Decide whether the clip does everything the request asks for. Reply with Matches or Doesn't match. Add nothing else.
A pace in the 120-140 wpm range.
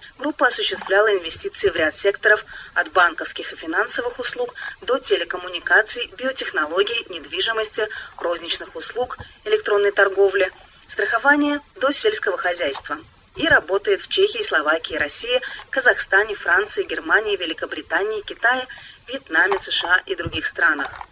Doesn't match